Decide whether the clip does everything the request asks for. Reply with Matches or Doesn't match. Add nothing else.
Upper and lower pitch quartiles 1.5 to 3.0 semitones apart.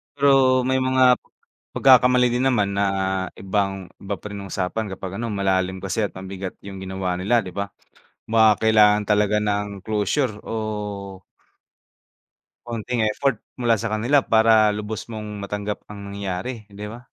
Matches